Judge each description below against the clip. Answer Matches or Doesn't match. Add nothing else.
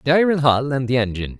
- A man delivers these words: Matches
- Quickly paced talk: Matches